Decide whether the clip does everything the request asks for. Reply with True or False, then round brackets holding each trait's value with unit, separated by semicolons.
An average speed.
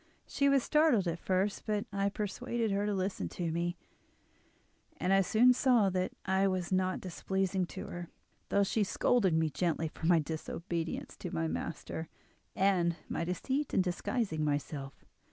True (160 wpm)